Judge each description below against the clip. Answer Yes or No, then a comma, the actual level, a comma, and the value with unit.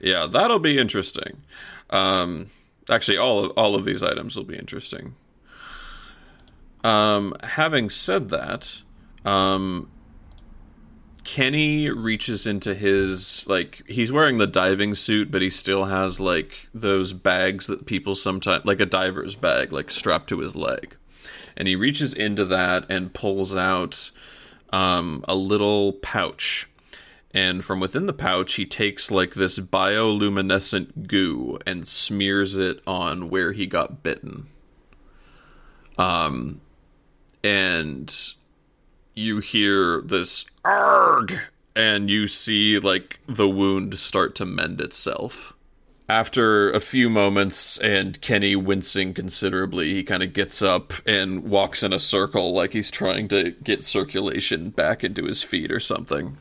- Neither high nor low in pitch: No, low, 100 Hz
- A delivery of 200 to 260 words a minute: No, slow, 135 wpm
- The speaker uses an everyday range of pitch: No, narrow, 2.0 semitones